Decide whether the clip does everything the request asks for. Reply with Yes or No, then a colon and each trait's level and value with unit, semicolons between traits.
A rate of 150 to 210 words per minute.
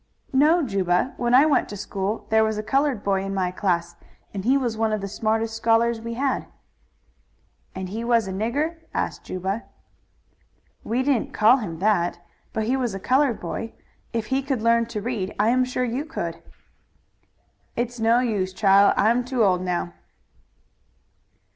Yes: average, 175 wpm